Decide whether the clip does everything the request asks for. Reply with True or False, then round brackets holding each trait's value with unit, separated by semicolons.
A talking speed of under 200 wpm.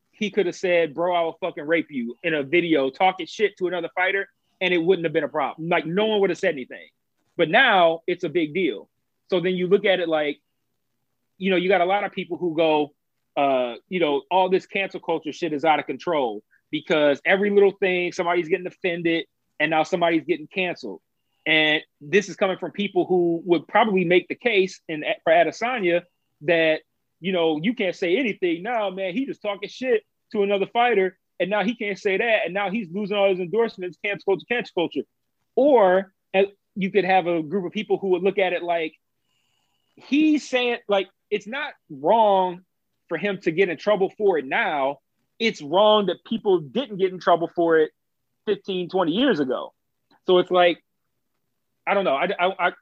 False (205 wpm)